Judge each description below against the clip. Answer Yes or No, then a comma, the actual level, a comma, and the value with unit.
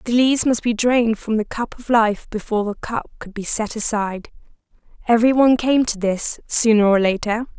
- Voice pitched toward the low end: No, high, 225 Hz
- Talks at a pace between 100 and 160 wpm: No, average, 200 wpm